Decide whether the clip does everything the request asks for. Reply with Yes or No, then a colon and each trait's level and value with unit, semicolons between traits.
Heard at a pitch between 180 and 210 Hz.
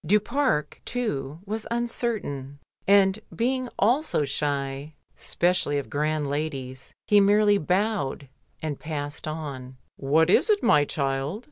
No: medium, 155 Hz